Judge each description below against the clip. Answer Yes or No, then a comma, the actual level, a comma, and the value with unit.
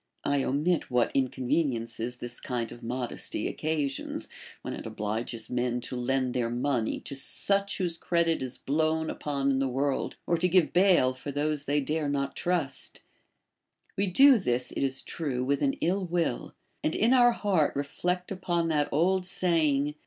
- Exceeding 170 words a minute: No, average, 165 wpm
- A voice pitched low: No, medium, 145 Hz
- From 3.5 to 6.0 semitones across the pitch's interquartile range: Yes, average, 5.2 semitones